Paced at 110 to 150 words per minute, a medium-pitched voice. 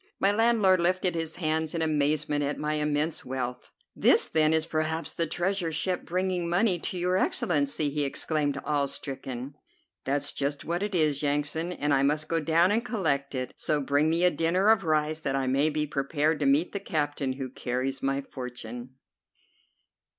No: average, 180 wpm; medium, 155 Hz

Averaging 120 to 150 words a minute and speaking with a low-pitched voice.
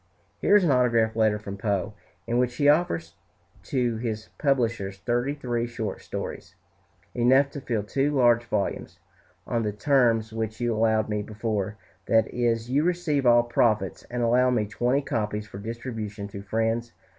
No: average, 165 wpm; low, 115 Hz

